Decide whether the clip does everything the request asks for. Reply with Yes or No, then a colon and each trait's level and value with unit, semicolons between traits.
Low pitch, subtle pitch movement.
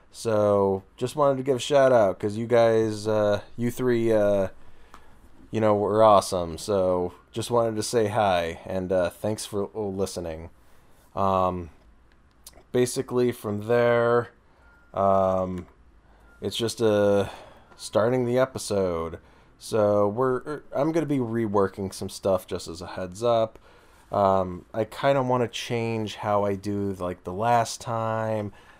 No: low, 105 Hz; average, 3.7 semitones